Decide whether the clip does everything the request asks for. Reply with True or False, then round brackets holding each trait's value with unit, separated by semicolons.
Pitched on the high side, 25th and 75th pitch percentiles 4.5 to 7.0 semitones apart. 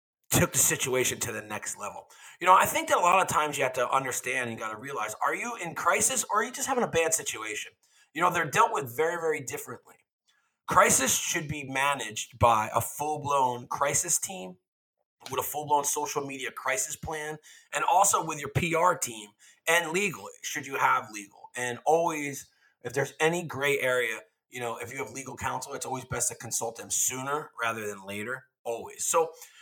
False (140 Hz; 5.1 semitones)